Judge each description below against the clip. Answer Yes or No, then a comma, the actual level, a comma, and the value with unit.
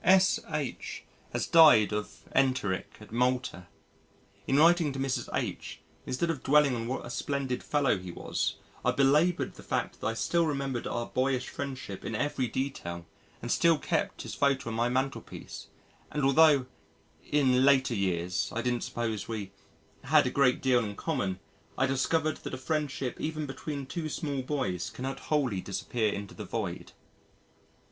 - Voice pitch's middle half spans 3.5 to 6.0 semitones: Yes, average, 4.0 semitones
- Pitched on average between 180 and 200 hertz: No, low, 130 Hz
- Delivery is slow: No, average, 160 wpm